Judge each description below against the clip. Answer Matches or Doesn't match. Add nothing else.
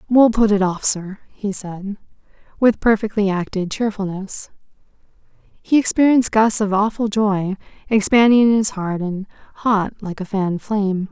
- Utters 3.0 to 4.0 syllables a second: Doesn't match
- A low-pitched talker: Doesn't match